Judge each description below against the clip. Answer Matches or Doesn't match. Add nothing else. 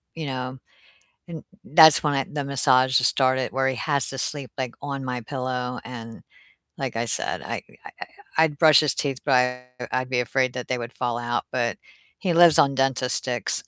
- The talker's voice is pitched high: Doesn't match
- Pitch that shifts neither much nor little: Doesn't match